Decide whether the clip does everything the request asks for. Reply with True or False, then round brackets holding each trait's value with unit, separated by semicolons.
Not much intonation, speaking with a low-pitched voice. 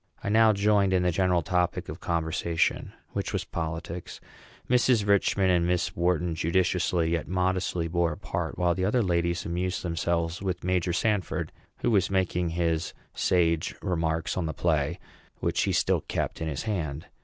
True (2.0 semitones; 90 Hz)